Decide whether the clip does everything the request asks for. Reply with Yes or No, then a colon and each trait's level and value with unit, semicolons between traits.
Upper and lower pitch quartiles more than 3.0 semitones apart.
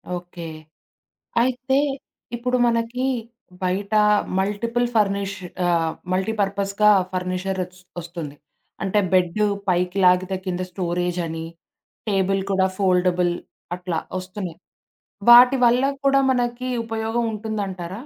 Yes: average, 3.7 semitones